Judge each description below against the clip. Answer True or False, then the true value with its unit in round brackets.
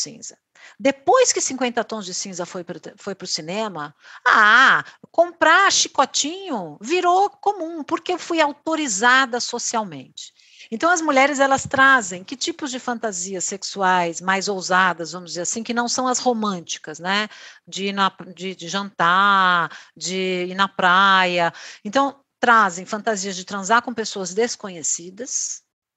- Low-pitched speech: False (220 Hz)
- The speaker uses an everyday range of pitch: False (6.8 semitones)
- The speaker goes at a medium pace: True (140 wpm)